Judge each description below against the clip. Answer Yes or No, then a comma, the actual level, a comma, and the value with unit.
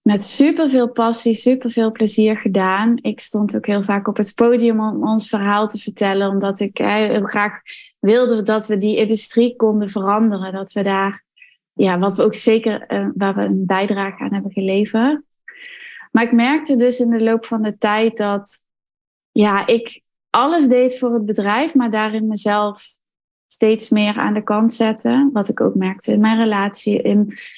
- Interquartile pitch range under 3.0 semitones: Yes, narrow, 2.4 semitones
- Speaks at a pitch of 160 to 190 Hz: No, high, 220 Hz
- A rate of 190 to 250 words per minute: No, average, 180 wpm